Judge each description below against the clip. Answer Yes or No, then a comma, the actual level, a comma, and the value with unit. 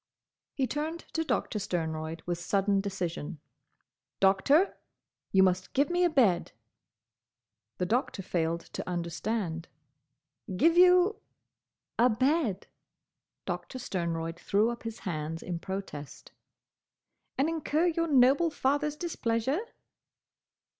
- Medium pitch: No, high, 215 Hz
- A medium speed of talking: No, slow, 110 wpm